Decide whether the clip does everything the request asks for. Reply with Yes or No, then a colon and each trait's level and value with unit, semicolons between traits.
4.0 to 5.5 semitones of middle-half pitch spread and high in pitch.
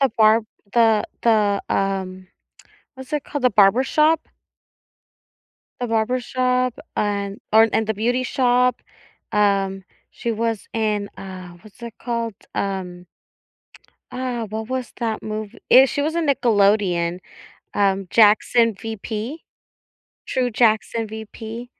No: average, 3.5 semitones; high, 220 Hz